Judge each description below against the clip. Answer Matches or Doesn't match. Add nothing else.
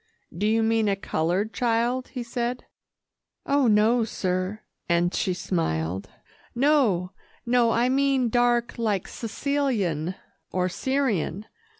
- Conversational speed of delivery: Doesn't match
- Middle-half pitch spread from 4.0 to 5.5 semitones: Matches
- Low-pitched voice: Doesn't match